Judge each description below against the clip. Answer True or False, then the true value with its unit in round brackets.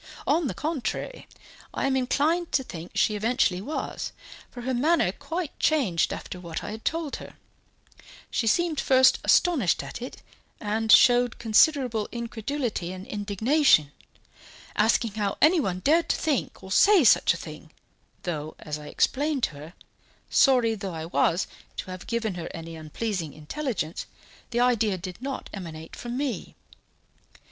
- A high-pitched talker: True (225 Hz)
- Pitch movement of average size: False (7.0 semitones)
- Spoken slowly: False (150 wpm)